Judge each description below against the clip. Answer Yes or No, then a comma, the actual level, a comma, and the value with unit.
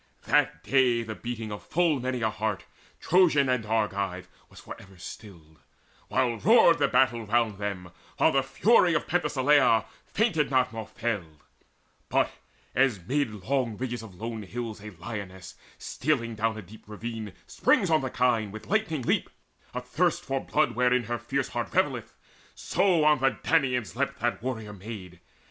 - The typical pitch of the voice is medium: No, low, 120 Hz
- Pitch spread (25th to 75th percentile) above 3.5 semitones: Yes, average, 4.2 semitones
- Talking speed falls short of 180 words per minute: Yes, average, 160 wpm